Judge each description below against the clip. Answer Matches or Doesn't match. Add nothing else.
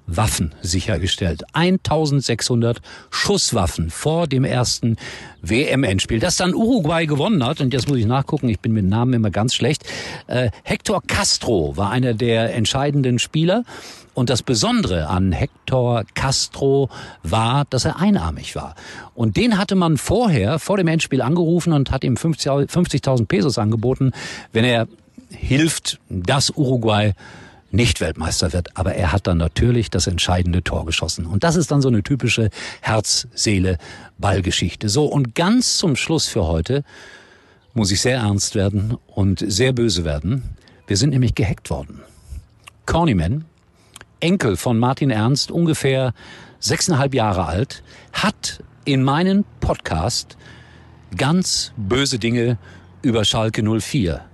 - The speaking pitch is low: Matches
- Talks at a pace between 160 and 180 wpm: Doesn't match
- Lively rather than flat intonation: Matches